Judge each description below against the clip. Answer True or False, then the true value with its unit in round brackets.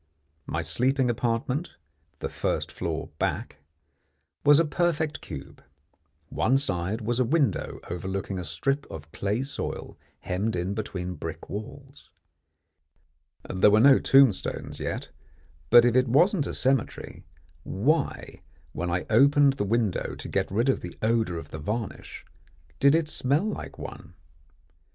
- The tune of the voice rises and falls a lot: True (6.3 semitones)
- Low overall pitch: True (120 Hz)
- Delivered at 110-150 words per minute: True (140 wpm)